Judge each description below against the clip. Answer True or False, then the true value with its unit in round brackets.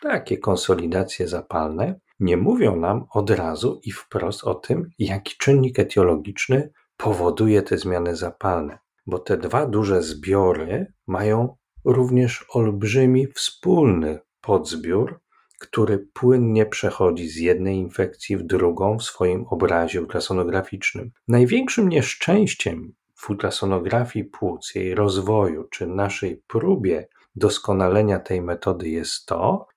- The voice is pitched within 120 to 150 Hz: False (100 Hz)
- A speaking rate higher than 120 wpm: False (115 wpm)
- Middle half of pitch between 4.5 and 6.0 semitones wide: True (4.8 semitones)